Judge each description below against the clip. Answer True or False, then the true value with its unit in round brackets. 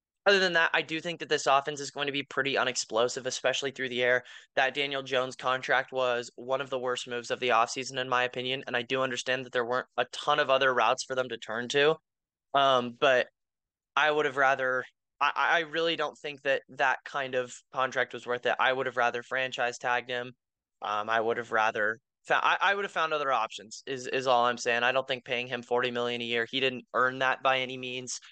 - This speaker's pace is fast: True (235 wpm)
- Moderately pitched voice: False (130 Hz)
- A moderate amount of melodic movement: False (1.9 semitones)